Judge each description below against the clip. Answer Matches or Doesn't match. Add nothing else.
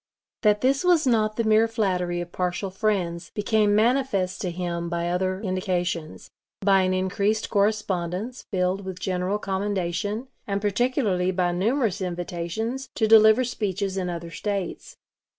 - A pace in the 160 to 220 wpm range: Doesn't match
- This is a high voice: Matches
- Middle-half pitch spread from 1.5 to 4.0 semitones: Matches